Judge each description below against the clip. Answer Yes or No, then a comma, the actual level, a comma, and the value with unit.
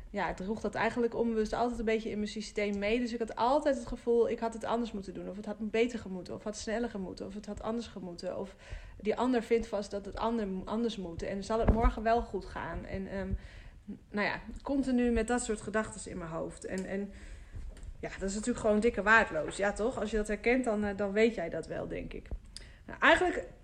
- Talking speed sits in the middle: No, fast, 245 wpm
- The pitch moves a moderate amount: No, narrow, 2.3 semitones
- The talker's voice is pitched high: Yes, high, 220 Hz